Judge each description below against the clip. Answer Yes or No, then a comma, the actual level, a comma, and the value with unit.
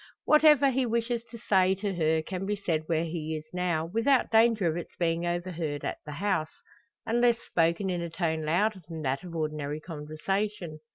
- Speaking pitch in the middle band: Yes, medium, 175 Hz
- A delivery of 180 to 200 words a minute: Yes, average, 185 wpm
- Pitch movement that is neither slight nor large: Yes, average, 4.8 semitones